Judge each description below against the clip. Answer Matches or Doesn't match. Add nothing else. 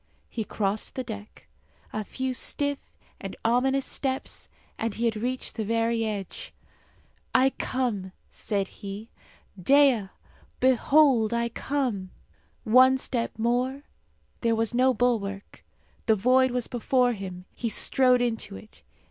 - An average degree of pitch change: Matches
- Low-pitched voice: Doesn't match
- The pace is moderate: Doesn't match